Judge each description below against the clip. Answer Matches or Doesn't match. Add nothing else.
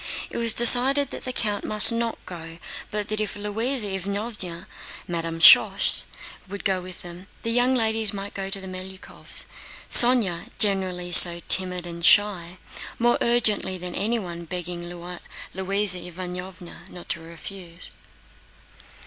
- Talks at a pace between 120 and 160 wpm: Matches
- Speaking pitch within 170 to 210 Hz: Matches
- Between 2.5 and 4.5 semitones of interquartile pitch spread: Matches